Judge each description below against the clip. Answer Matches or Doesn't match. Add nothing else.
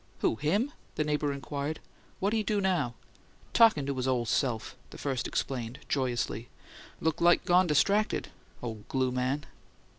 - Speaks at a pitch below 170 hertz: Matches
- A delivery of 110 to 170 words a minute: Matches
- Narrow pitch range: Doesn't match